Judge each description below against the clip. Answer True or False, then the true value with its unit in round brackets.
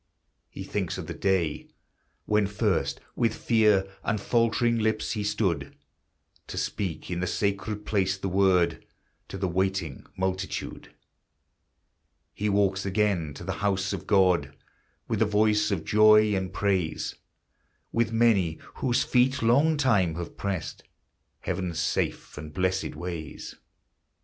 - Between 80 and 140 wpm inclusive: True (135 wpm)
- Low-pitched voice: True (95 Hz)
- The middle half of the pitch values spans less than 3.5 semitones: True (2.8 semitones)